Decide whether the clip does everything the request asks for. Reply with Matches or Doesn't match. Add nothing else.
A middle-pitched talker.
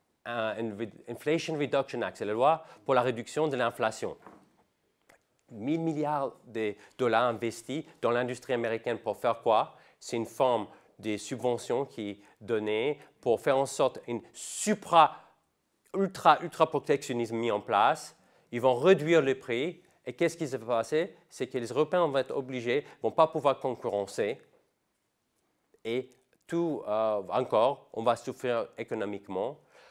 Doesn't match